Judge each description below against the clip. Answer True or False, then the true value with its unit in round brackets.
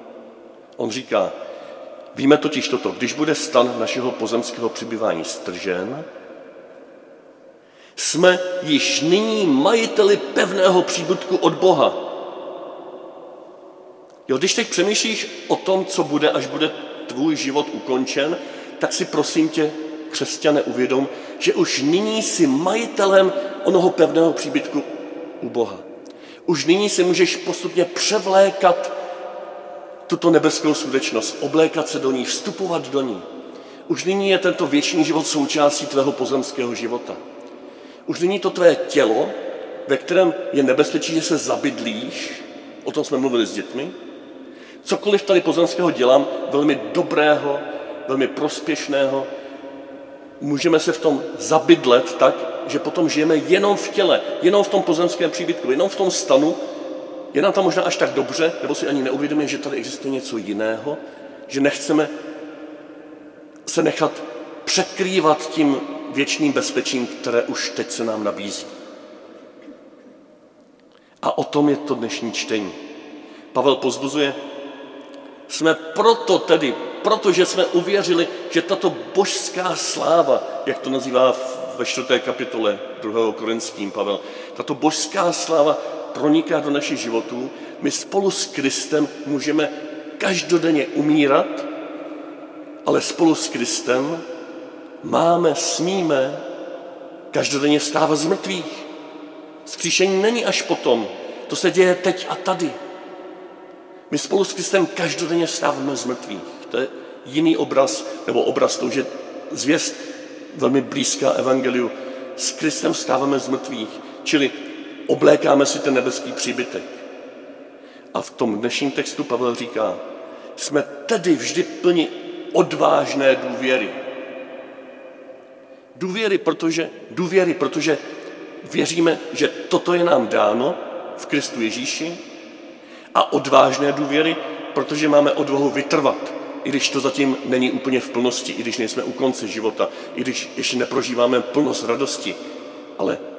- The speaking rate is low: False (125 wpm)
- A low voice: False (165 Hz)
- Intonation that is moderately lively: False (5.9 semitones)